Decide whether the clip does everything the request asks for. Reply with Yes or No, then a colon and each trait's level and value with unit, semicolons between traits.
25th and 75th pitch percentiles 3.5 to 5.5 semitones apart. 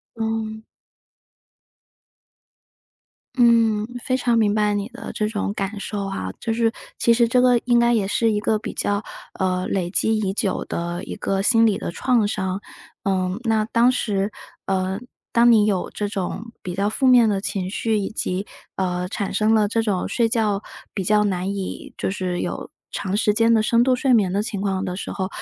No: average, 2.8 semitones